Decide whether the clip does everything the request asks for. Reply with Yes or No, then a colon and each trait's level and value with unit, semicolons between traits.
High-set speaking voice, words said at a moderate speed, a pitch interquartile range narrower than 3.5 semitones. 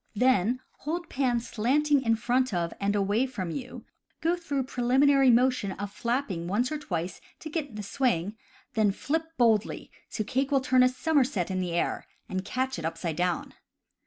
No: high, 245 Hz; average, 175 wpm; wide, 5.4 semitones